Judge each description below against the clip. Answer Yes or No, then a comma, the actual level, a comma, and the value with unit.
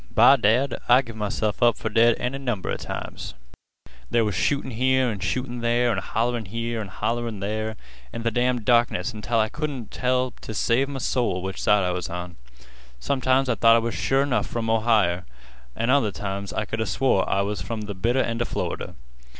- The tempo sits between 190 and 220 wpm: Yes, fast, 205 wpm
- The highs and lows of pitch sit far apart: No, average, 2.9 semitones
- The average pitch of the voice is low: Yes, low, 115 Hz